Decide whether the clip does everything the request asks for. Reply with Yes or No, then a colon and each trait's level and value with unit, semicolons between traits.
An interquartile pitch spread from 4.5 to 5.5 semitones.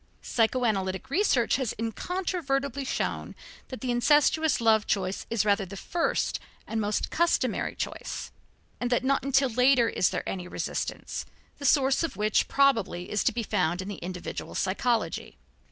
Yes: average, 5.1 semitones